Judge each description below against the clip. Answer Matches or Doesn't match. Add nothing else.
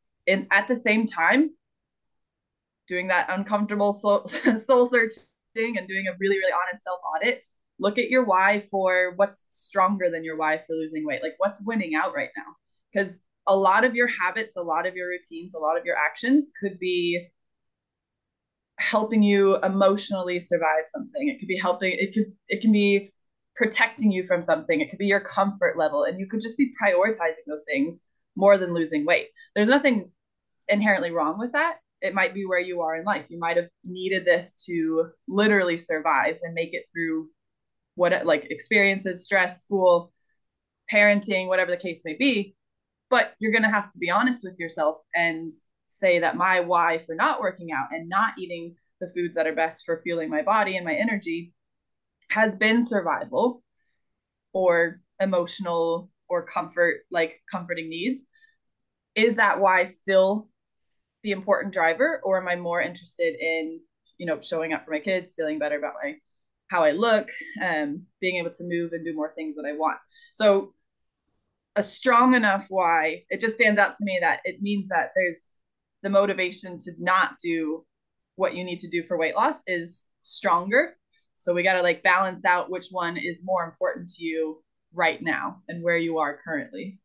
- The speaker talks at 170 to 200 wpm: Matches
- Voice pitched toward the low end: Doesn't match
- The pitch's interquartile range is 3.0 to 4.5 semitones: Matches